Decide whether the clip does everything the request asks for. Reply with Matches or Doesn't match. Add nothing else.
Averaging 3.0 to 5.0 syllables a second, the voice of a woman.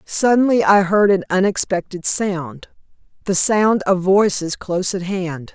Matches